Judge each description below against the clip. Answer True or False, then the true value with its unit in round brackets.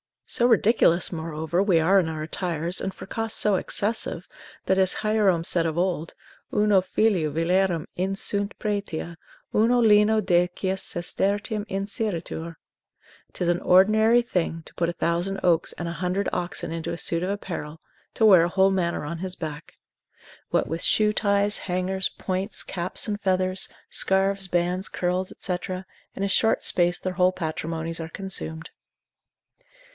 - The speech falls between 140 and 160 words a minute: True (155 wpm)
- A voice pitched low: False (185 Hz)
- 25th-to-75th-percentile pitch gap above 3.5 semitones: False (3.0 semitones)